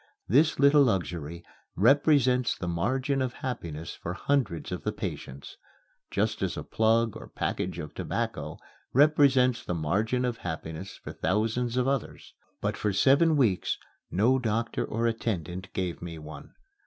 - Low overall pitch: Yes, low, 115 Hz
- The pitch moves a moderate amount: No, wide, 6.9 semitones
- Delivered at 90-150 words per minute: Yes, average, 145 wpm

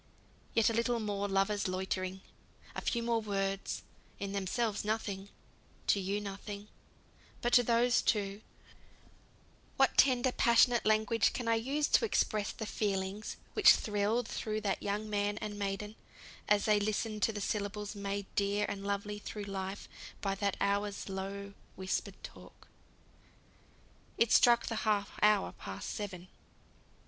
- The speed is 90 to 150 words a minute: Yes, average, 140 wpm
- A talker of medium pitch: No, high, 205 Hz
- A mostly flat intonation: Yes, narrow, 1.7 semitones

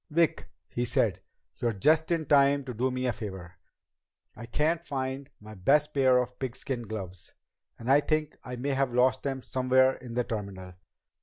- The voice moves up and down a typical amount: Yes, average, 3.2 semitones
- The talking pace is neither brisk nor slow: Yes, average, 175 wpm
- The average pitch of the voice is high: No, low, 130 Hz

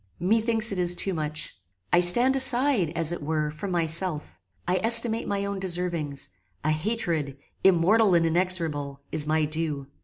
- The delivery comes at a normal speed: Yes, average, 155 wpm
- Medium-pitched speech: Yes, medium, 175 Hz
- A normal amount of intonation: Yes, average, 4.5 semitones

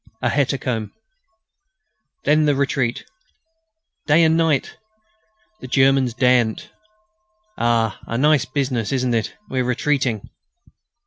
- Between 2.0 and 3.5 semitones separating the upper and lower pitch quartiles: Yes, average, 3.1 semitones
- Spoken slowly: Yes, slow, 105 wpm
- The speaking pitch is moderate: No, low, 130 Hz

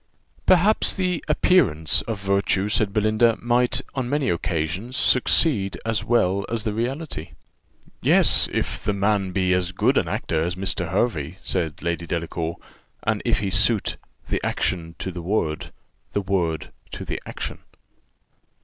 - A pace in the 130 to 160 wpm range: Yes, average, 150 wpm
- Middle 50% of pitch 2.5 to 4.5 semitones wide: No, wide, 5.4 semitones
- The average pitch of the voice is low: Yes, low, 100 Hz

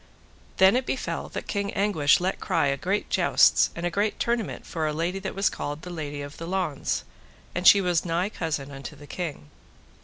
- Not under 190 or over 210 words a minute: Yes, fast, 205 wpm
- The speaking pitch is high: No, medium, 175 Hz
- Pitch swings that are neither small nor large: Yes, average, 4.5 semitones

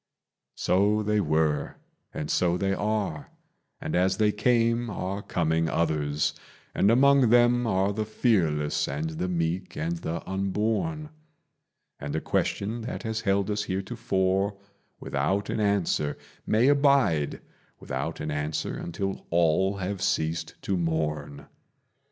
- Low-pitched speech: Yes, very low, 95 Hz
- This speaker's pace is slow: Yes, slow, 130 wpm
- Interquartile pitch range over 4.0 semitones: Yes, average, 5.1 semitones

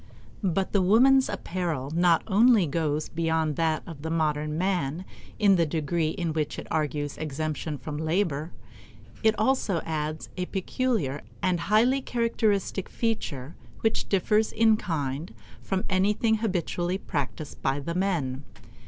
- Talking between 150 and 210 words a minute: No, slow, 135 wpm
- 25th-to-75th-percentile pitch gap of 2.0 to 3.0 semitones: No, average, 4.8 semitones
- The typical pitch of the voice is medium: Yes, medium, 170 Hz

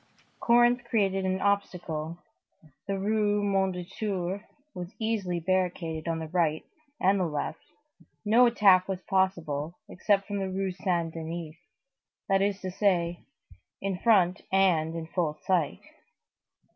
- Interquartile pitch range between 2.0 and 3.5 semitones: Yes, average, 2.8 semitones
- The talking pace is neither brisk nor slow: No, slow, 130 wpm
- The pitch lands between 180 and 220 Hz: Yes, medium, 185 Hz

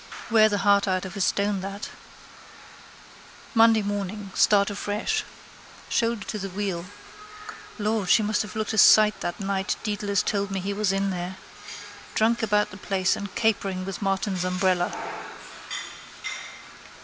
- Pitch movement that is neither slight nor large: No, narrow, 1.9 semitones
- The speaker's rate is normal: Yes, average, 145 wpm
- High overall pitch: Yes, high, 200 Hz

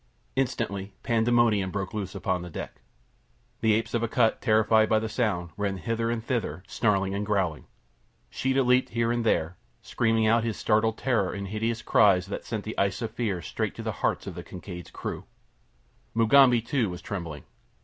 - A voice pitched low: Yes, low, 110 Hz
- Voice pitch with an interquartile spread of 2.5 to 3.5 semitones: Yes, average, 3.0 semitones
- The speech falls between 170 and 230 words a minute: Yes, average, 180 wpm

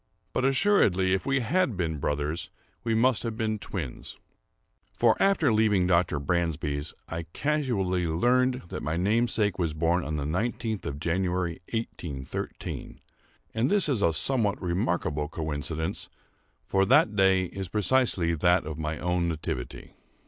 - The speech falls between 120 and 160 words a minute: Yes, average, 140 wpm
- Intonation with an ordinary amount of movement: No, wide, 5.8 semitones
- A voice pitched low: Yes, very low, 90 Hz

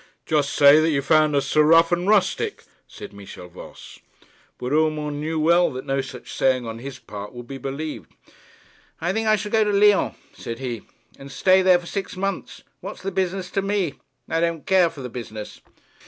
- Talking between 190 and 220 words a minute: Yes, average, 200 wpm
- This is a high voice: No, medium, 155 Hz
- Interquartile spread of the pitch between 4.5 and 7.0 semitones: Yes, wide, 5.6 semitones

